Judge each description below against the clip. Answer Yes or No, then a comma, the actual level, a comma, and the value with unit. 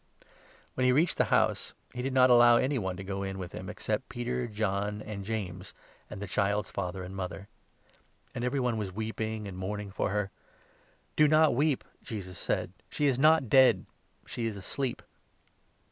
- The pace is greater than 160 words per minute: Yes, average, 190 wpm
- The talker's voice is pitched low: Yes, low, 110 Hz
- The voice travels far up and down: No, average, 4.4 semitones